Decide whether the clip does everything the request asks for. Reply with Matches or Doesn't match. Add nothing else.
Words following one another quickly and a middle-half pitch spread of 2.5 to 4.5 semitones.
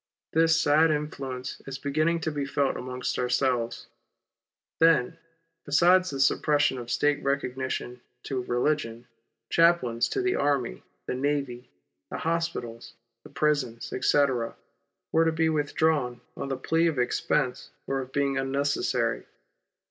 Doesn't match